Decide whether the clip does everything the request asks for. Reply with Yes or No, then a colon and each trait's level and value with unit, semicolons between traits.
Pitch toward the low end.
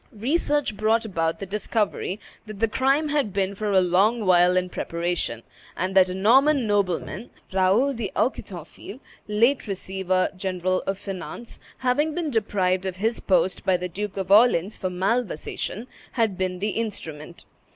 No: high, 195 Hz